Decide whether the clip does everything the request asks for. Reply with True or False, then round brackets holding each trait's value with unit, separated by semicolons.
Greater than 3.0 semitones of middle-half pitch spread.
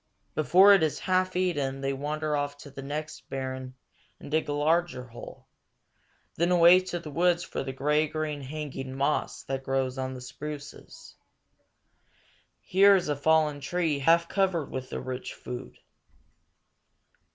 True (4.0 semitones)